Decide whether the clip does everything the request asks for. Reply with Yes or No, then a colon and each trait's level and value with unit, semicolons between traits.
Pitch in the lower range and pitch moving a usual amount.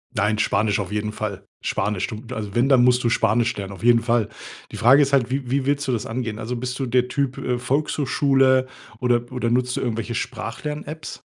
Yes: low, 120 Hz; average, 3.0 semitones